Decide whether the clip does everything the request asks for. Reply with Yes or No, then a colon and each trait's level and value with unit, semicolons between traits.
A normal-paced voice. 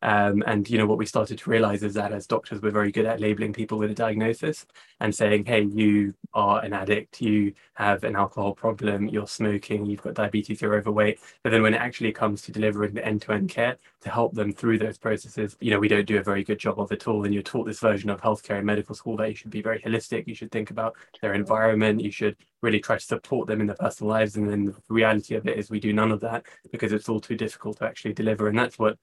No: fast, 260 wpm